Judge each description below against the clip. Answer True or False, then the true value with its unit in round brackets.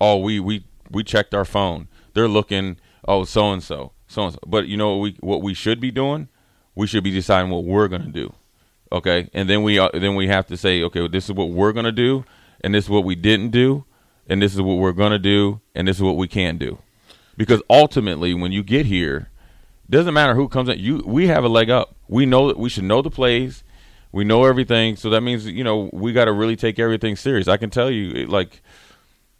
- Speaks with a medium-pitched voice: False (105 Hz)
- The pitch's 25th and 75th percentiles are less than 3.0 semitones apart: False (3.5 semitones)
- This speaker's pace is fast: True (240 wpm)